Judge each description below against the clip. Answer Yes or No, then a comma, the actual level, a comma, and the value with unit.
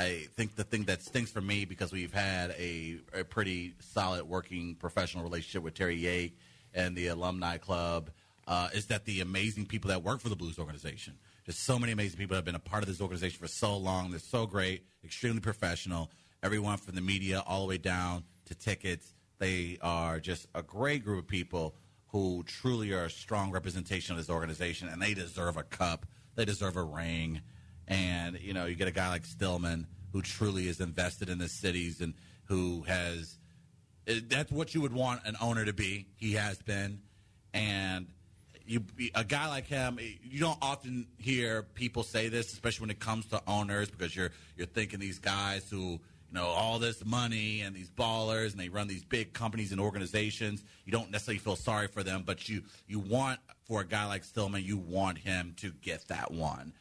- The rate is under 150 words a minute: No, average, 200 wpm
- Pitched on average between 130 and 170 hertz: No, very low, 95 Hz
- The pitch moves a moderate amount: Yes, average, 3.3 semitones